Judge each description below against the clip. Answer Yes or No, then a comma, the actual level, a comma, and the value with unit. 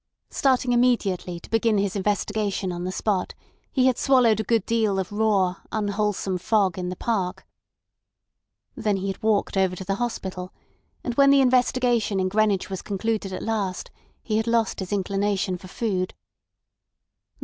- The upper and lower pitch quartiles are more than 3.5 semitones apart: No, average, 3.1 semitones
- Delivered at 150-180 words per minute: Yes, average, 160 wpm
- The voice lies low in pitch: No, high, 205 Hz